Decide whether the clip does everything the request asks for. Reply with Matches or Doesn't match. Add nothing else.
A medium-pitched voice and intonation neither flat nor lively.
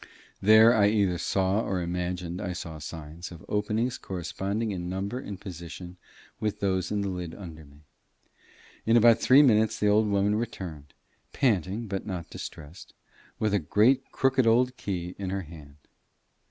Doesn't match